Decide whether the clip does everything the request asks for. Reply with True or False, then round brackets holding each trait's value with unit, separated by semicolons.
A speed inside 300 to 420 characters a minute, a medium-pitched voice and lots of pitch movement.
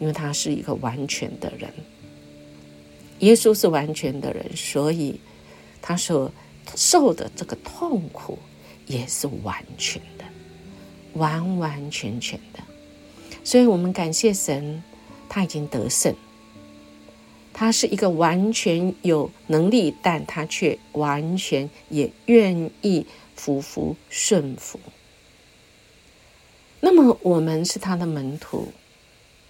False (160 characters per minute; 155 Hz; 8.7 semitones)